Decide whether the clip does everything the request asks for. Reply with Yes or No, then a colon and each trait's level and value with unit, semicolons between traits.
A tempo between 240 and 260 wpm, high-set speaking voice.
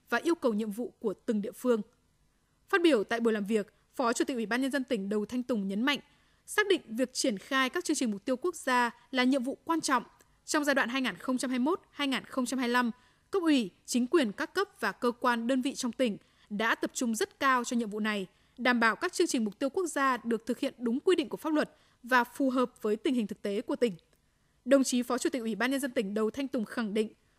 Yes: fast, 250 wpm; very high, 250 Hz